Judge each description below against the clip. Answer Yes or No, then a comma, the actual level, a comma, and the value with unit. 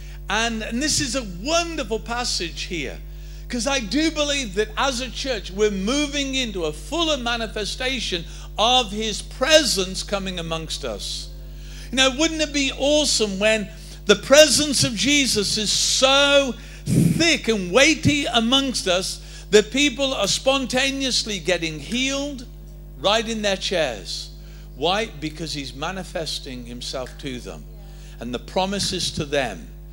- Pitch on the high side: Yes, high, 215 Hz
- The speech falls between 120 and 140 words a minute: Yes, slow, 135 wpm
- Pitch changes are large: Yes, wide, 8.7 semitones